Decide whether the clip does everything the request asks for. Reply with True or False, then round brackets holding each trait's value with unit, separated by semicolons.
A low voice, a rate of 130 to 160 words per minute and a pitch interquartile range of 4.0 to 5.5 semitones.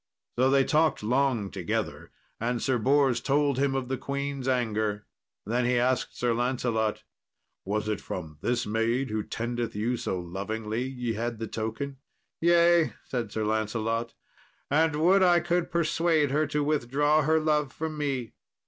True (125 Hz; 155 wpm; 4.6 semitones)